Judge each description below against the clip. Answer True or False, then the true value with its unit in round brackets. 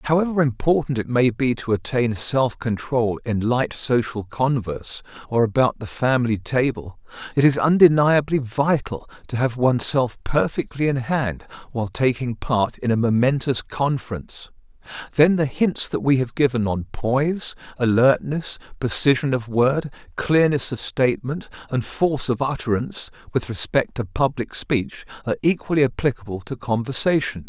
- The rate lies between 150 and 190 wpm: False (140 wpm)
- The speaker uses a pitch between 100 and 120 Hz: False (130 Hz)